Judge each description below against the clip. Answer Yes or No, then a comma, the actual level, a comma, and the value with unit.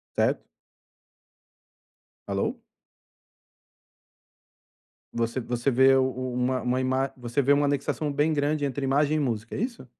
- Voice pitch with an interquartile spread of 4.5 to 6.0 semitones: No, narrow, 2.4 semitones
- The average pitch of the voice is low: Yes, low, 130 Hz